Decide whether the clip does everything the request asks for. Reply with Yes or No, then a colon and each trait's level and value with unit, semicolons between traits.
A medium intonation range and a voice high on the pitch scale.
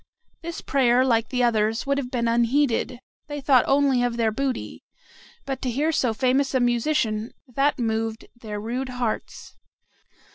Yes: average, 3.0 semitones; high, 245 Hz